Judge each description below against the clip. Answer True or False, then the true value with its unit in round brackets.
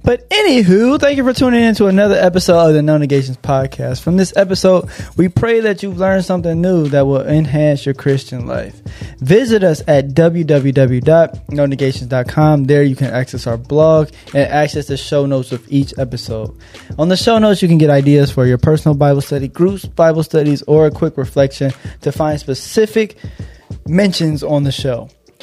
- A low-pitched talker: False (150 Hz)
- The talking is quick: False (180 wpm)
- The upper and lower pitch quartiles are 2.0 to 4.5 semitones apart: False (4.9 semitones)